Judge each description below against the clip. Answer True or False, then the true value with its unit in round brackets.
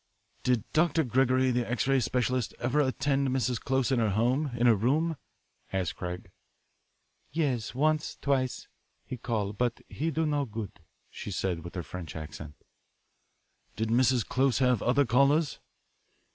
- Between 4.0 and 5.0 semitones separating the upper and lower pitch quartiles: False (3.6 semitones)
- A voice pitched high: False (125 Hz)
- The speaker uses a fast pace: False (150 wpm)